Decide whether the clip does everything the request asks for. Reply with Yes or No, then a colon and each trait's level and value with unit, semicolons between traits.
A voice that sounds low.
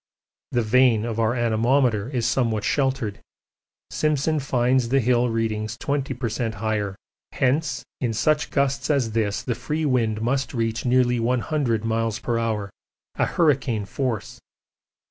Yes: low, 120 Hz